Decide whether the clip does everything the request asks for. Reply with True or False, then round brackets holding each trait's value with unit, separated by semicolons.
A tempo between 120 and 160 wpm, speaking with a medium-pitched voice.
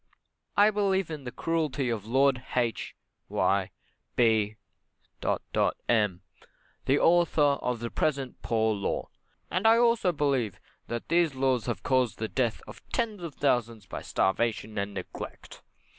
False (140 wpm; 130 Hz)